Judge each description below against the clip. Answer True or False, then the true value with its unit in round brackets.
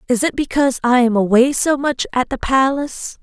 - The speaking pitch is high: True (255 Hz)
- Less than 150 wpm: False (205 wpm)